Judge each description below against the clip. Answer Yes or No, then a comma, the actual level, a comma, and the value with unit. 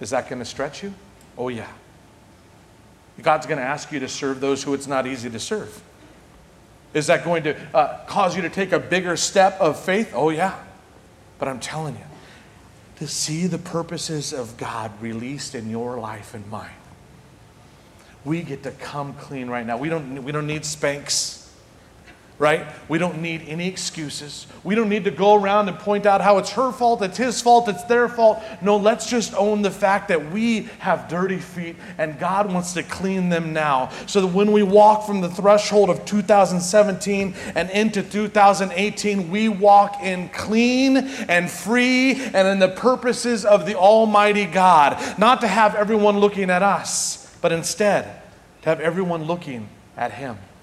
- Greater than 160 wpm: Yes, average, 180 wpm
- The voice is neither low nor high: Yes, medium, 180 Hz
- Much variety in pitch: Yes, wide, 6.2 semitones